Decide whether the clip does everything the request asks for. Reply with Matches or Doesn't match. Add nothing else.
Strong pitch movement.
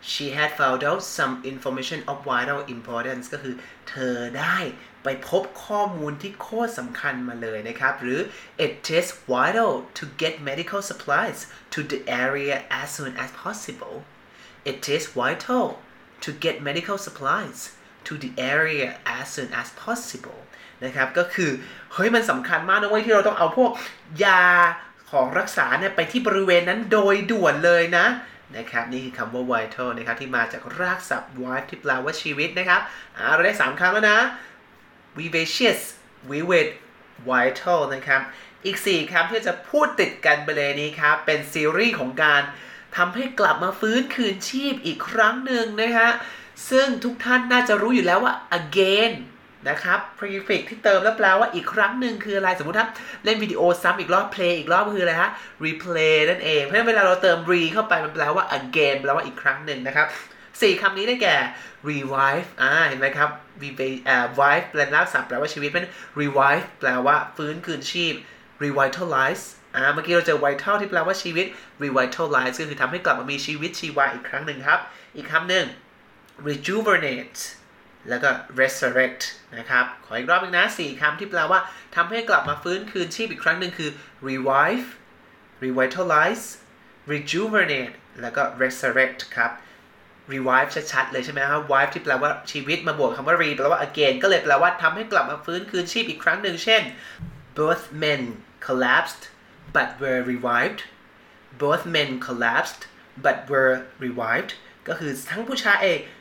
Matches